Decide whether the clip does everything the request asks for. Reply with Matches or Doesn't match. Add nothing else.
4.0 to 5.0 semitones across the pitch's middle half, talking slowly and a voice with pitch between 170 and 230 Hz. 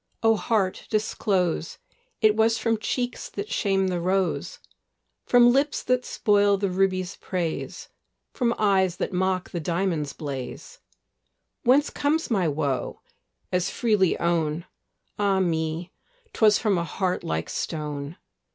Matches